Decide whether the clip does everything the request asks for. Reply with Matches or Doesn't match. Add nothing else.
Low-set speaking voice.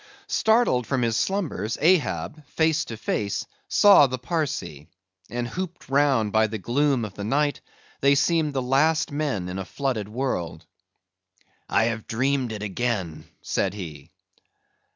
Matches